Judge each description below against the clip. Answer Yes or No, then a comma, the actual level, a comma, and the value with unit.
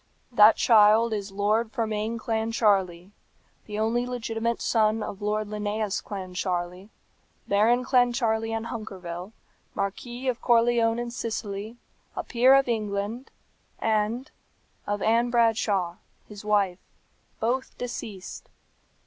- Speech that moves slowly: Yes, slow, 110 wpm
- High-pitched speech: Yes, high, 220 Hz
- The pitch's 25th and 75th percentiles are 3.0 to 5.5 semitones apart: No, narrow, 2.4 semitones